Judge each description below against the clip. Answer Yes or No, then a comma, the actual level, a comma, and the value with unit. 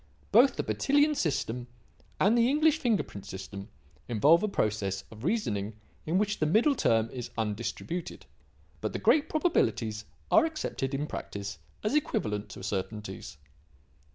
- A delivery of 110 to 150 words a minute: Yes, average, 140 wpm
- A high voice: No, low, 135 Hz